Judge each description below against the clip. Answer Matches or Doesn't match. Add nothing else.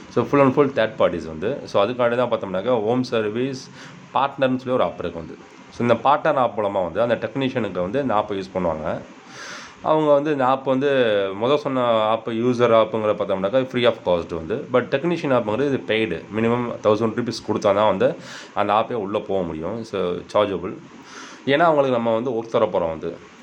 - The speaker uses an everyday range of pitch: Matches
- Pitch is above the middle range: Doesn't match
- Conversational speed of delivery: Doesn't match